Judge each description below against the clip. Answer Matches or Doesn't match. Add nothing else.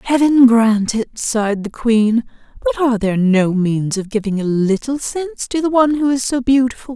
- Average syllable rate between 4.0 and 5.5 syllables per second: Matches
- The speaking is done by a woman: Matches